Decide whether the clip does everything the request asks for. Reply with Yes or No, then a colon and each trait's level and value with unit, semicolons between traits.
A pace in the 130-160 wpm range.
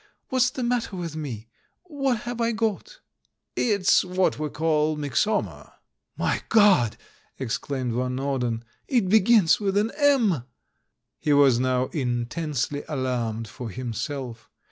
Yes: average, 140 wpm